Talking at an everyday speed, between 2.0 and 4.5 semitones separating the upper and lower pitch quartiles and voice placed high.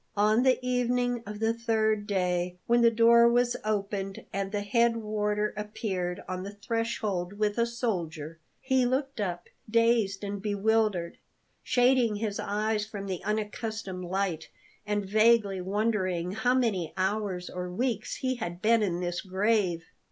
Yes: average, 150 wpm; average, 3.4 semitones; high, 210 Hz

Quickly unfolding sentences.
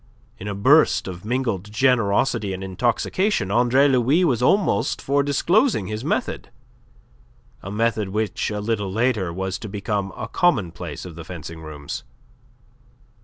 No: average, 140 wpm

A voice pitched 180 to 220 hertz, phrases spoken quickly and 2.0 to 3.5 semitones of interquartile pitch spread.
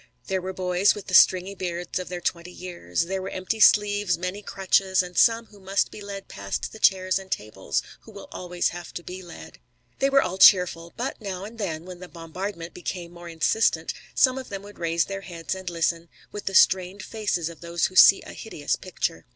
Yes: medium, 185 Hz; fast, 215 wpm; narrow, 2.5 semitones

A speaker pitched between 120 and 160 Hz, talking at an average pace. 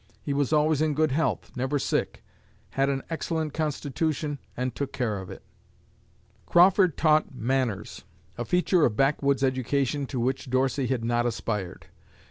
Yes: low, 135 Hz; average, 150 wpm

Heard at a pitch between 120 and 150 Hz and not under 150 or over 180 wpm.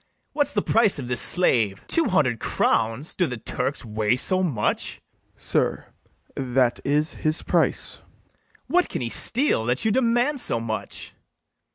Yes: low, 135 Hz; average, 160 wpm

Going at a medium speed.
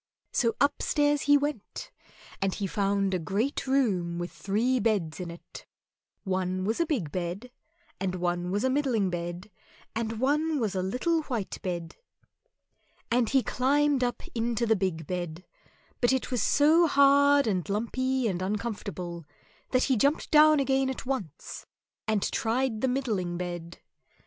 Yes: average, 155 wpm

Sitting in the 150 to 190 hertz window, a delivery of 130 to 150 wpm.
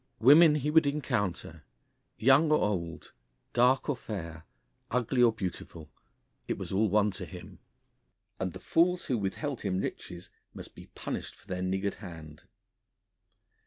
No: low, 105 Hz; average, 145 wpm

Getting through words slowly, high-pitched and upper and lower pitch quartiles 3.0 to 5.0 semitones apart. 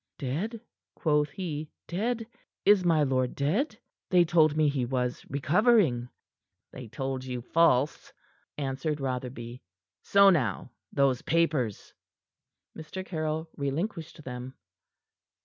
No: slow, 110 wpm; medium, 150 Hz; average, 4.7 semitones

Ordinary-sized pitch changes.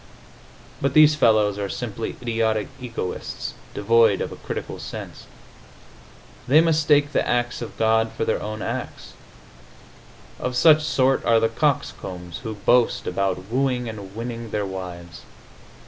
Yes: average, 3.7 semitones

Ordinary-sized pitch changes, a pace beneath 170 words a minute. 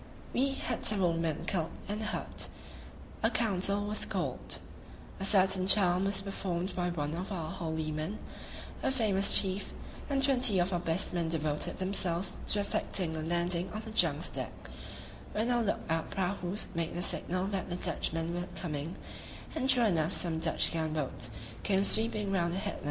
No: average, 3.3 semitones; average, 175 wpm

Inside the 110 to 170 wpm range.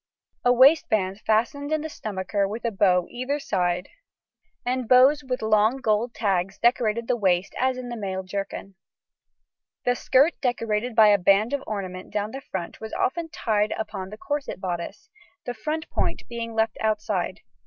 Yes: average, 165 wpm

